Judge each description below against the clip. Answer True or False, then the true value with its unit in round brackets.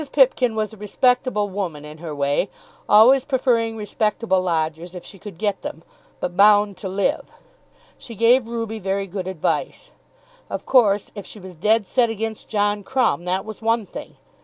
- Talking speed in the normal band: True (170 wpm)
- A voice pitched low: False (205 Hz)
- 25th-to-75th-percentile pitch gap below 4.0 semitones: True (3.3 semitones)